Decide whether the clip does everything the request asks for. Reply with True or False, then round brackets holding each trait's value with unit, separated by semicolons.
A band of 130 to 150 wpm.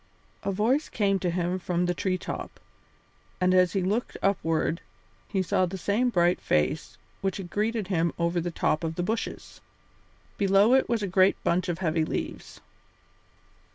False (170 wpm)